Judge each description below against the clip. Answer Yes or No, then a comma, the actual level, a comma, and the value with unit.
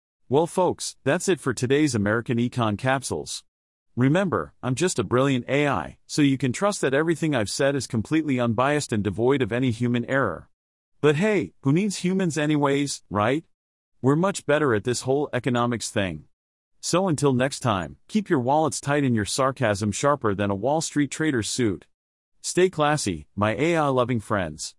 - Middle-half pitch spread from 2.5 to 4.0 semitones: No, average, 5.3 semitones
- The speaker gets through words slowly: No, average, 170 wpm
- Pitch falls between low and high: No, low, 130 Hz